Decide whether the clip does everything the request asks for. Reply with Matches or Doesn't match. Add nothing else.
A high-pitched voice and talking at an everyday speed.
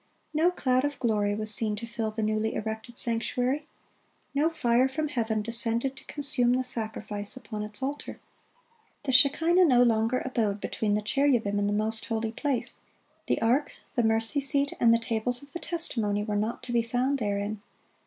Matches